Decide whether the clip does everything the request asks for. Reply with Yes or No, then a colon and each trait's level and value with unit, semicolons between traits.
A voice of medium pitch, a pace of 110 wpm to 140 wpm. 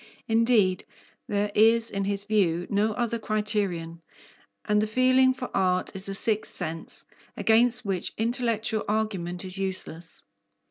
No: high, 210 Hz; slow, 135 wpm